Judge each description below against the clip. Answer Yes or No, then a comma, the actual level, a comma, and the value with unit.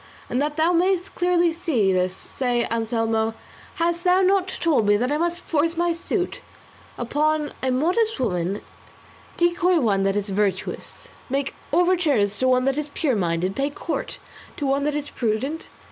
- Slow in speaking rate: No, average, 165 wpm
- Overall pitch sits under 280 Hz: No, very high, 285 Hz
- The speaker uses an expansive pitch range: Yes, wide, 7.3 semitones